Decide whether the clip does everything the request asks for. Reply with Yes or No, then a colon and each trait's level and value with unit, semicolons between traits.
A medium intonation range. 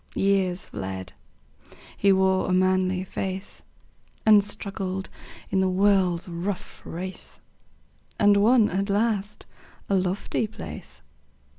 No: narrow, 1.5 semitones